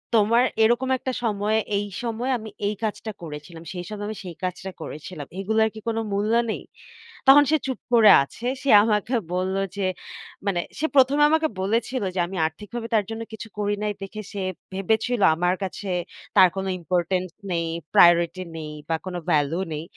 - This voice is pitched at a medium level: No, high, 205 Hz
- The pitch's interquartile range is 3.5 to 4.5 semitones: Yes, average, 3.9 semitones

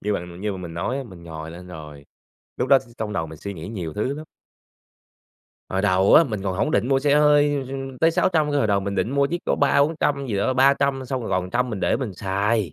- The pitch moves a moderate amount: No, wide, 6.9 semitones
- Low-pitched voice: Yes, low, 110 Hz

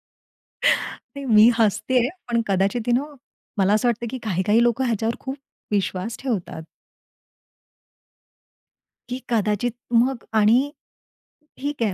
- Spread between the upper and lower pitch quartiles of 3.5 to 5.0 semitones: No, average, 3.1 semitones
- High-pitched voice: Yes, high, 230 Hz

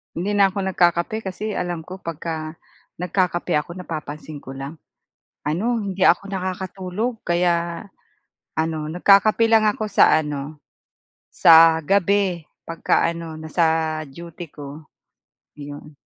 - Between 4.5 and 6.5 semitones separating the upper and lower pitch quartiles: No, average, 3.4 semitones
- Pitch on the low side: No, medium, 170 Hz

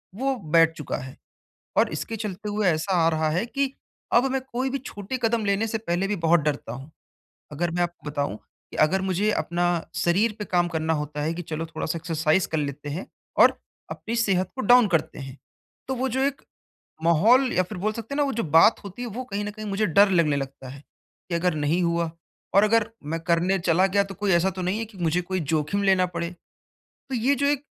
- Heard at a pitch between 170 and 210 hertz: Yes, medium, 185 Hz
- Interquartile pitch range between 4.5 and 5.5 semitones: Yes, average, 4.9 semitones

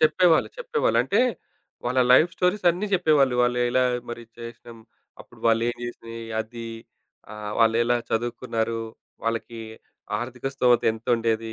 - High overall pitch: No, low, 120 Hz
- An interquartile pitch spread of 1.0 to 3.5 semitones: Yes, average, 2.8 semitones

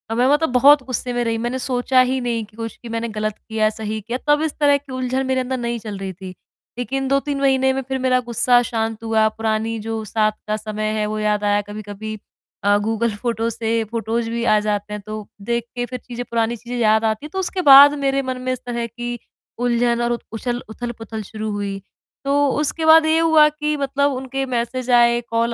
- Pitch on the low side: No, high, 235 Hz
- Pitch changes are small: No, average, 3.0 semitones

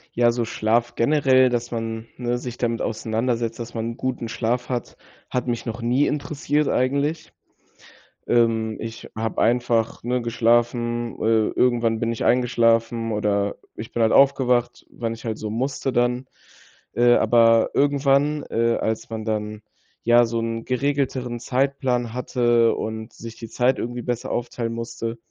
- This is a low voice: Yes, low, 120 Hz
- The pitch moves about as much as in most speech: No, narrow, 1.6 semitones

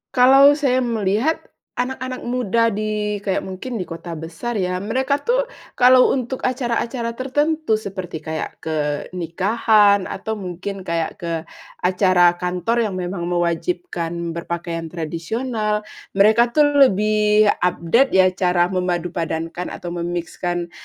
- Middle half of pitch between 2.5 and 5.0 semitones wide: No, wide, 5.4 semitones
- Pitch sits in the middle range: No, high, 200 Hz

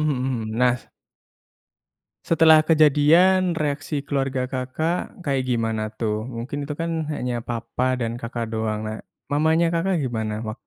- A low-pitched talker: Yes, low, 130 Hz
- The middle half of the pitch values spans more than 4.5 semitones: Yes, average, 5.1 semitones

